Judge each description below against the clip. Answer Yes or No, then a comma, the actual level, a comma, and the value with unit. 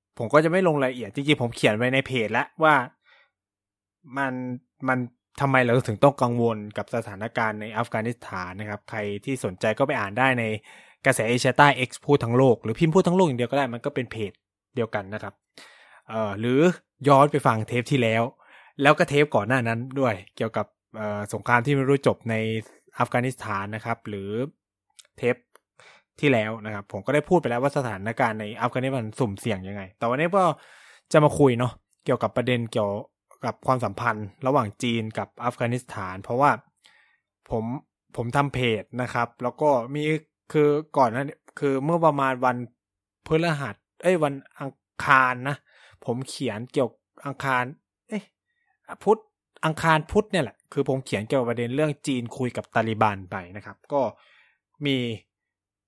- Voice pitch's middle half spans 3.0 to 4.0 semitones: No, average, 4.4 semitones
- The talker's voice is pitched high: No, low, 125 Hz